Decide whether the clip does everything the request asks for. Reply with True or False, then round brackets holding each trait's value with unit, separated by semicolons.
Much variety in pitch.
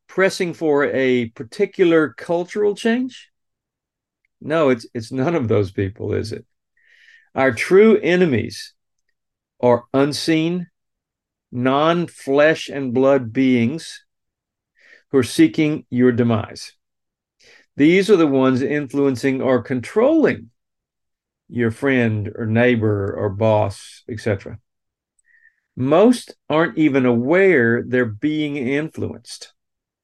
True (6.0 semitones)